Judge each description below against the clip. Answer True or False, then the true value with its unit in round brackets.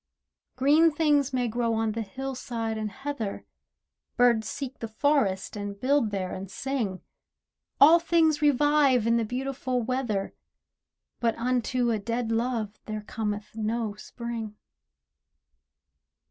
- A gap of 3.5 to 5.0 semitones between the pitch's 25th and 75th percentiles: True (3.8 semitones)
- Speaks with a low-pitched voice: False (235 Hz)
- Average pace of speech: False (125 wpm)